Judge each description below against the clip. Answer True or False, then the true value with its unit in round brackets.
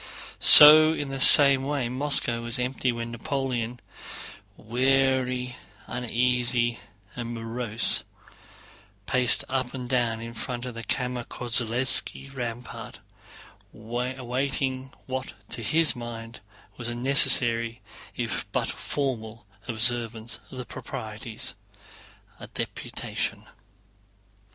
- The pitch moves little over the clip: True (2.1 semitones)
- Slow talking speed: True (100 wpm)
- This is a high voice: False (125 Hz)